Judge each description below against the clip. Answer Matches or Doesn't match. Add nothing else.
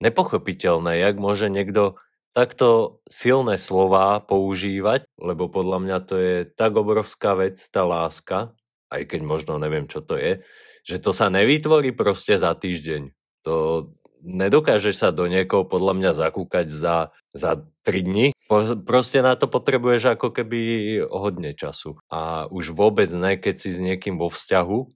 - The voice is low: Matches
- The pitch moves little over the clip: Doesn't match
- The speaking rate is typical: Matches